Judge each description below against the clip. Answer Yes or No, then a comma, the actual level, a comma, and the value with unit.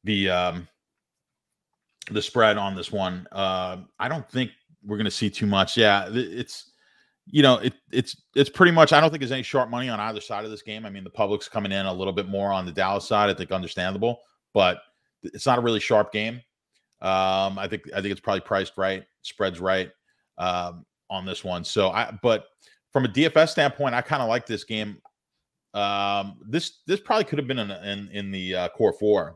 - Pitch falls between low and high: No, low, 105 Hz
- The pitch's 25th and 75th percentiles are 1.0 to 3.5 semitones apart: No, average, 4.4 semitones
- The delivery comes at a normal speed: No, fast, 215 wpm